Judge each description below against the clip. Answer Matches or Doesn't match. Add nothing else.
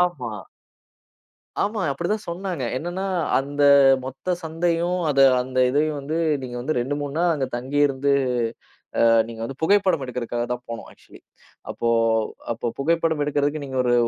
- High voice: Doesn't match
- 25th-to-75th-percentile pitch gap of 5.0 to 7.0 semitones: Doesn't match